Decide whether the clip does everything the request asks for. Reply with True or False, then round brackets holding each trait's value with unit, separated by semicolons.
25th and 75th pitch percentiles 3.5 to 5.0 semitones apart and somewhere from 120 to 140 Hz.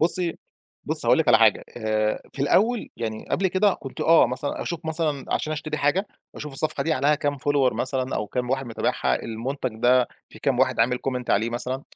True (3.9 semitones; 135 Hz)